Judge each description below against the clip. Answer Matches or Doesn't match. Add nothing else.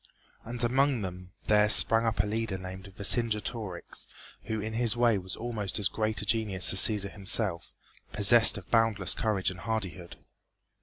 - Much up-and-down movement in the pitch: Doesn't match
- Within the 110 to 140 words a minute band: Doesn't match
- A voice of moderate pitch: Doesn't match